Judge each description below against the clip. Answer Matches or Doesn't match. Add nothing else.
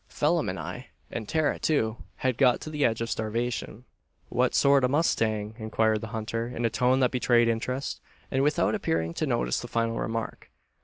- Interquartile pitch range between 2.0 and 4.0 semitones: Matches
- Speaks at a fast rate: Doesn't match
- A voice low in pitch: Matches